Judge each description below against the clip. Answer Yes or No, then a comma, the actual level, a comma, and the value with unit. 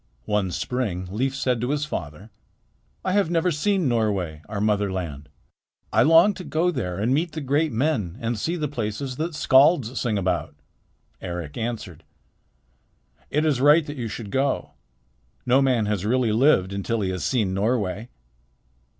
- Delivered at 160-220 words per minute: Yes, average, 165 wpm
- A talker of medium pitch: No, low, 120 Hz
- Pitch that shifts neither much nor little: No, wide, 6.5 semitones